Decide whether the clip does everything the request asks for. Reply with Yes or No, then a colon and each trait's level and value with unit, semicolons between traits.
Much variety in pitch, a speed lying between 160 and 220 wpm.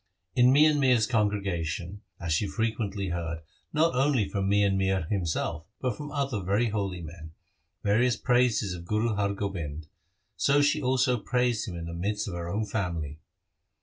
Yes: wide, 5.9 semitones; average, 165 wpm